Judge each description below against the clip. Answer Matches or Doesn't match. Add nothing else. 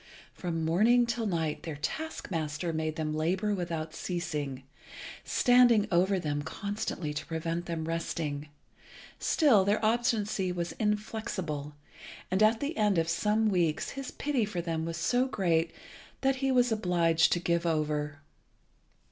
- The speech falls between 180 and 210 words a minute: Doesn't match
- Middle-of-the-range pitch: Matches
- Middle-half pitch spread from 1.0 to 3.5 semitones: Doesn't match